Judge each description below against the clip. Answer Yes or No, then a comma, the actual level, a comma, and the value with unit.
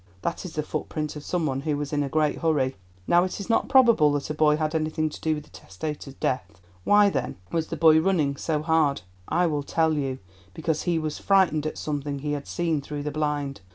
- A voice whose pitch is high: No, medium, 155 Hz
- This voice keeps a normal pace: No, fast, 230 wpm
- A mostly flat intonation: Yes, narrow, 1.9 semitones